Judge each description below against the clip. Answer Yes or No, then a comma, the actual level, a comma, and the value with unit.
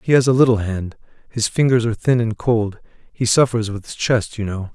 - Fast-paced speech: Yes, fast, 215 wpm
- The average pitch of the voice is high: No, low, 115 Hz